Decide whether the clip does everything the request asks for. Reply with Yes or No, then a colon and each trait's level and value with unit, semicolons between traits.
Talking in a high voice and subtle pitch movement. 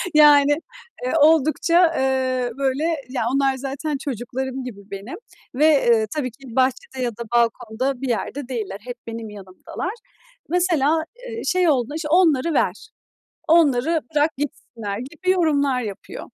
No: very high, 270 Hz; average, 4.3 semitones